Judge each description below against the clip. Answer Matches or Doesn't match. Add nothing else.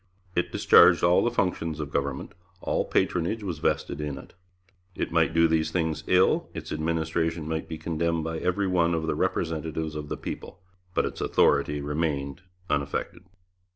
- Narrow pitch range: Matches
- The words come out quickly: Doesn't match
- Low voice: Matches